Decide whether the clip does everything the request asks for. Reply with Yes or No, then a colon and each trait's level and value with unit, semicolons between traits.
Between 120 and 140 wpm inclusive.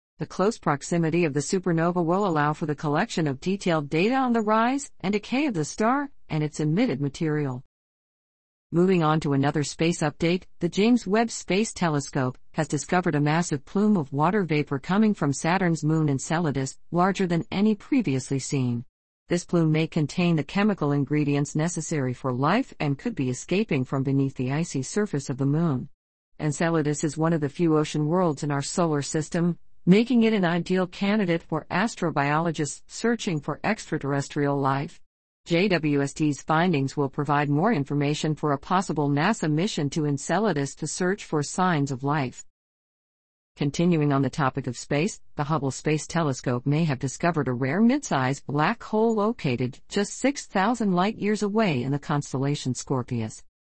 No: average, 165 wpm